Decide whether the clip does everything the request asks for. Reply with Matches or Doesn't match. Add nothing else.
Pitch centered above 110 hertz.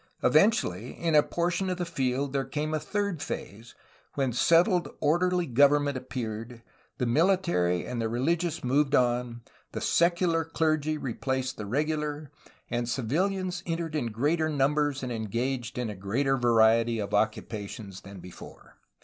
Matches